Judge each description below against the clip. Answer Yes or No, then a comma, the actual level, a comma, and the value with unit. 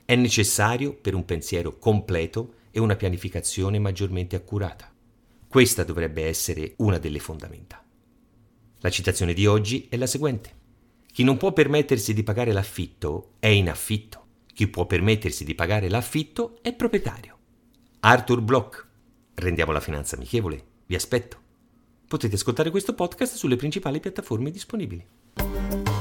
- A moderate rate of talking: Yes, average, 135 wpm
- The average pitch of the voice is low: Yes, low, 110 Hz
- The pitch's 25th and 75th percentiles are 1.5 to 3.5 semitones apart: No, average, 4.9 semitones